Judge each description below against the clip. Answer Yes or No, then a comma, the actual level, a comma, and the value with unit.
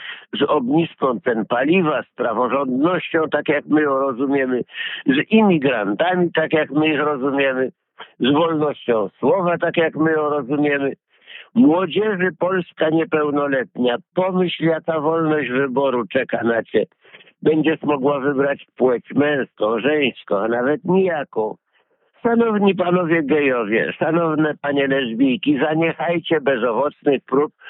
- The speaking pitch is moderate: Yes, medium, 155 Hz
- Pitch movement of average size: Yes, average, 3.7 semitones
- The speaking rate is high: No, average, 120 wpm